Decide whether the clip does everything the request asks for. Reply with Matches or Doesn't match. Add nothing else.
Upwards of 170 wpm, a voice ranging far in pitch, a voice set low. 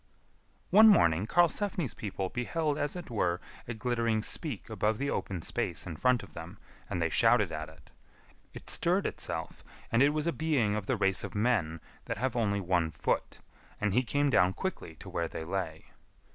Matches